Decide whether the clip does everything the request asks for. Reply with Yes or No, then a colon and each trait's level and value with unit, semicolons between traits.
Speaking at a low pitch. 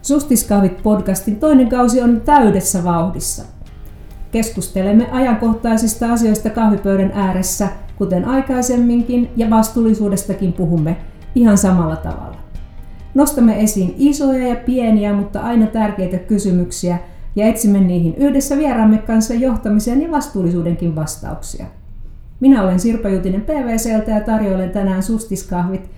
No: high, 210 Hz